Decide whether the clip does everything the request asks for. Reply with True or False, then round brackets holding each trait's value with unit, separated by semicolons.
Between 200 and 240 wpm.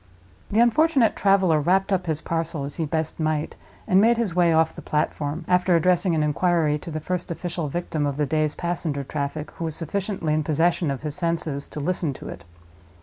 True (205 wpm)